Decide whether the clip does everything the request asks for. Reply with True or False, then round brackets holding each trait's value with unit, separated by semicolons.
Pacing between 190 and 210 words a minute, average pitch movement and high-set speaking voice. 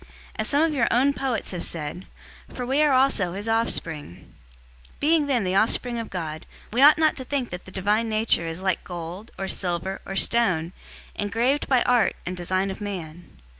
False (195 wpm; 6.0 semitones; 205 Hz)